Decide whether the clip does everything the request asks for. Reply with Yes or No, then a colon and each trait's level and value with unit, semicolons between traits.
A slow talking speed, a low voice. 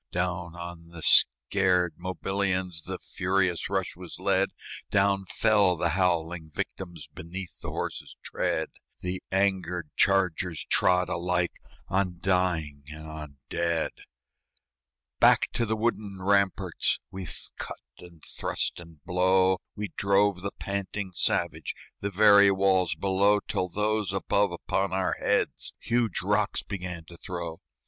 Yes: slow, 130 wpm; very low, 90 Hz